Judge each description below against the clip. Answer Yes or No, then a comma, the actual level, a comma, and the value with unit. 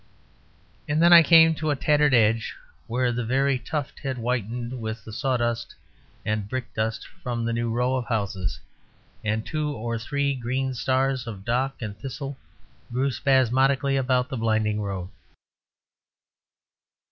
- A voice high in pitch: No, low, 125 Hz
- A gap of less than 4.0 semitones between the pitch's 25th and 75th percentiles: Yes, average, 3.1 semitones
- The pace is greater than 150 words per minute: No, average, 145 wpm